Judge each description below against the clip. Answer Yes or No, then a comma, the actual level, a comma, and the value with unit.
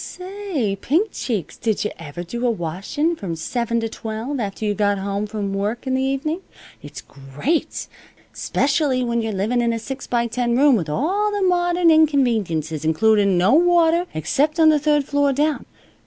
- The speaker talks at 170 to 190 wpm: Yes, average, 180 wpm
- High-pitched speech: Yes, high, 240 Hz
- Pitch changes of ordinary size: No, wide, 7.0 semitones